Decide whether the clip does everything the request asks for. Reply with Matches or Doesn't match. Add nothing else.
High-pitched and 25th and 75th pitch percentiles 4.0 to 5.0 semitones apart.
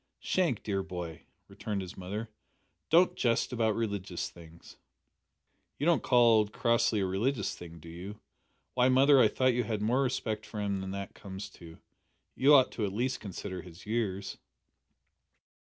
Doesn't match